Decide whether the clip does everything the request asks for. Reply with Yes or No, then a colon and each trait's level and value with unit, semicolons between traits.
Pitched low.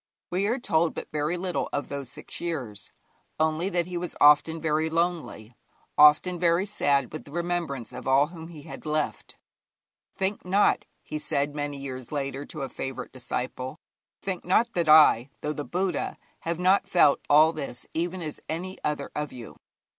No: medium, 155 Hz